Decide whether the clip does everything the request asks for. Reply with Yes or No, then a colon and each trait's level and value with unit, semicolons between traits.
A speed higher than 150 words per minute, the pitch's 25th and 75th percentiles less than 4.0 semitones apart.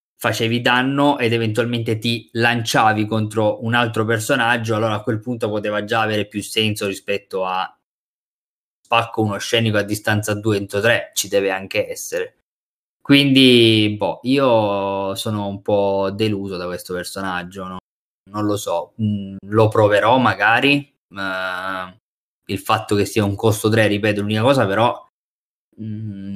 No: average, 145 wpm; average, 2.7 semitones